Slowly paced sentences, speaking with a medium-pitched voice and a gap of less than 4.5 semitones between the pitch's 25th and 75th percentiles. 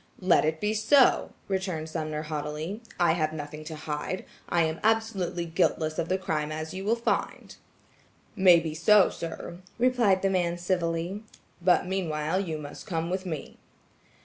No: average, 155 wpm; medium, 170 Hz; average, 3.3 semitones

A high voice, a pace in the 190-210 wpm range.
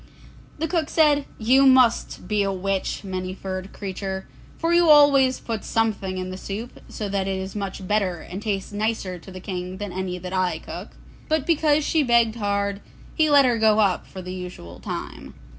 Yes: high, 200 Hz; average, 195 wpm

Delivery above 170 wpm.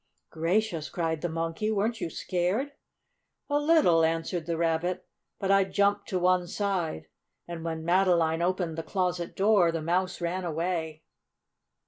No: average, 145 wpm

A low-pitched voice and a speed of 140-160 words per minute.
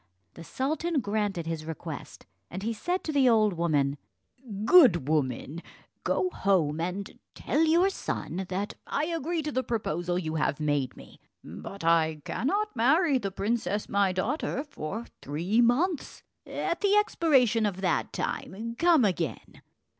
No: high, 210 Hz; average, 145 wpm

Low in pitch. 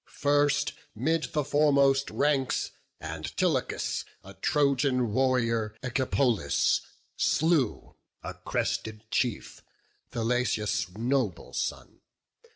Yes: low, 130 Hz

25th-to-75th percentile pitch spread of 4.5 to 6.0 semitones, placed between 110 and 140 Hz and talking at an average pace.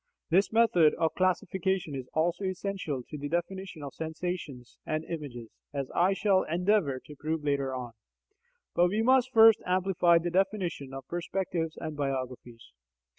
No: average, 4.9 semitones; medium, 170 Hz; average, 150 wpm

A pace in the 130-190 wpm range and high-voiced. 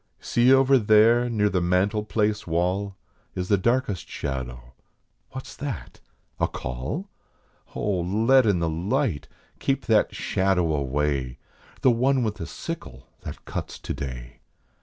No: average, 140 wpm; low, 100 Hz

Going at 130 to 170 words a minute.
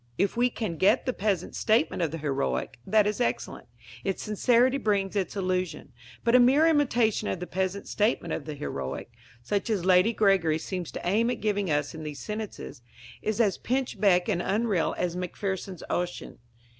No: average, 180 wpm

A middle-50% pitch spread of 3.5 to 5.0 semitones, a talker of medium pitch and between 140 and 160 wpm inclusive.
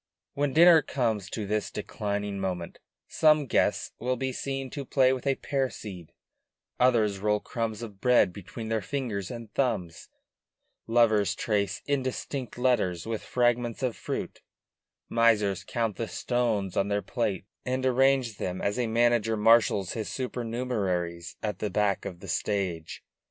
No: average, 3.9 semitones; low, 115 Hz; average, 150 wpm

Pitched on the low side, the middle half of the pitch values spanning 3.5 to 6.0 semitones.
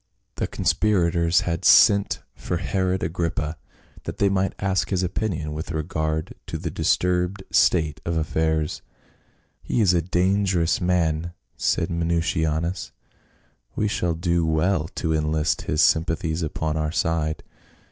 No: very low, 85 Hz; narrow, 2.5 semitones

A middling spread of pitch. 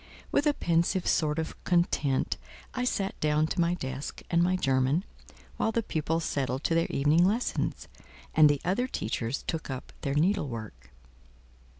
Yes: average, 4.5 semitones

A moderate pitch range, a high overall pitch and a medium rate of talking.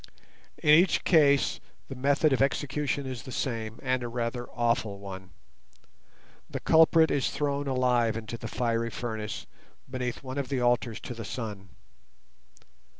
No: average, 3.4 semitones; low, 125 Hz; average, 150 wpm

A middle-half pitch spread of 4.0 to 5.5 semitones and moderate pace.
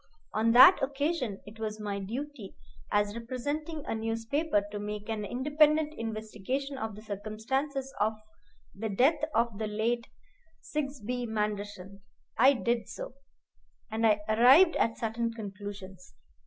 No: average, 4.3 semitones; slow, 130 wpm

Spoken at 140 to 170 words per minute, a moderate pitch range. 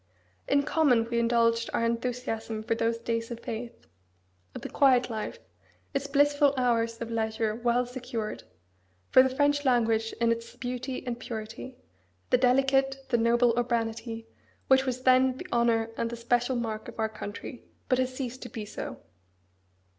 No: average, 160 wpm; narrow, 2.1 semitones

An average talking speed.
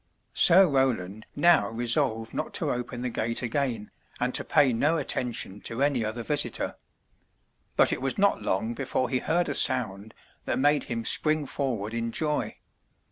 Yes: average, 165 wpm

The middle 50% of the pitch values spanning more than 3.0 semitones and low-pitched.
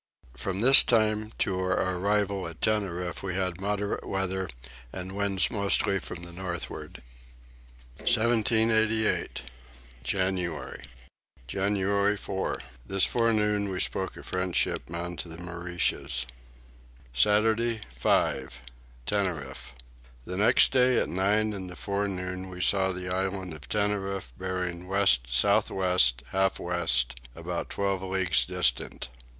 No: narrow, 2.6 semitones; very low, 95 Hz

